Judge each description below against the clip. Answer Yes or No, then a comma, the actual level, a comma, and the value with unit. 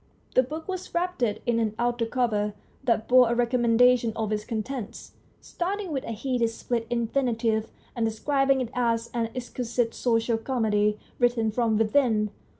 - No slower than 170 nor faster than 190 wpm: No, average, 150 wpm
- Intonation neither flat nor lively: No, narrow, 2.1 semitones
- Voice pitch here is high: Yes, high, 235 Hz